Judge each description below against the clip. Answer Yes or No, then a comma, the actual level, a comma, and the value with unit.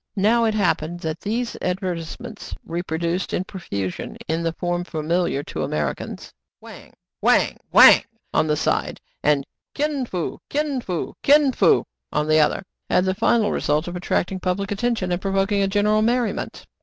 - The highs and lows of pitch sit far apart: No, average, 4.6 semitones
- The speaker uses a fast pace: No, average, 170 wpm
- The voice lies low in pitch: No, medium, 185 Hz